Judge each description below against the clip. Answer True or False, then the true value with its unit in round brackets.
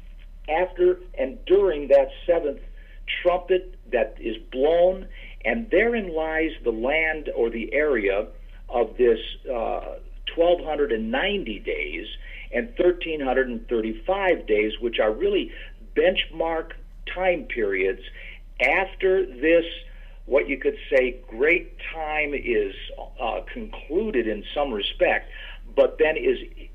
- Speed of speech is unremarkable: False (125 wpm)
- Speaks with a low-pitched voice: False (190 Hz)